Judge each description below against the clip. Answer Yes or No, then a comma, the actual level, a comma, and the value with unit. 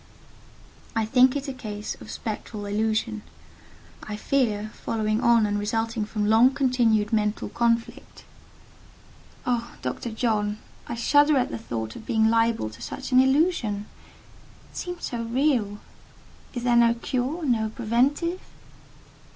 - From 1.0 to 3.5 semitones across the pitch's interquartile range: Yes, average, 3.0 semitones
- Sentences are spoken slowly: Yes, slow, 130 wpm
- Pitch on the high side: Yes, high, 230 Hz